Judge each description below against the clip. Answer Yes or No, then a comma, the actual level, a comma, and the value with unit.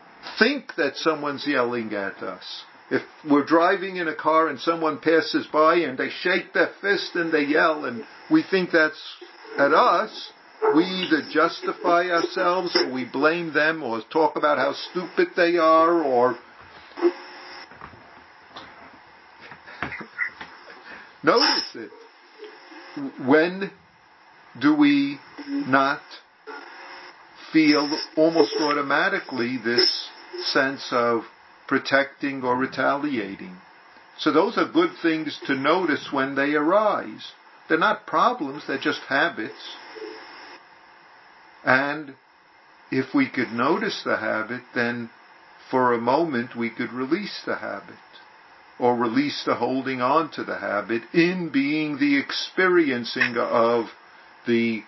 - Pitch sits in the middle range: Yes, medium, 160 Hz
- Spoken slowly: Yes, slow, 115 wpm